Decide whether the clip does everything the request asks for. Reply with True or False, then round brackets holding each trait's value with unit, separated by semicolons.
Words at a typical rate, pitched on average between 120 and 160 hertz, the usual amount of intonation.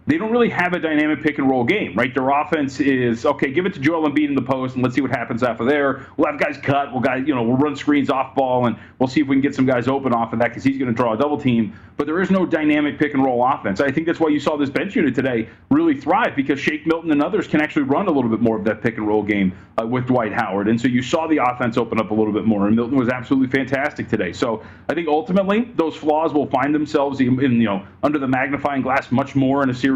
False (295 wpm; 135 Hz; 3.4 semitones)